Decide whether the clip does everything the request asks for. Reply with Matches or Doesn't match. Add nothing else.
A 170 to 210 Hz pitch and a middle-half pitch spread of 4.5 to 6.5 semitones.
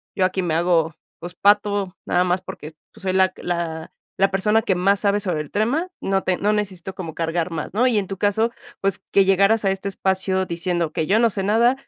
Doesn't match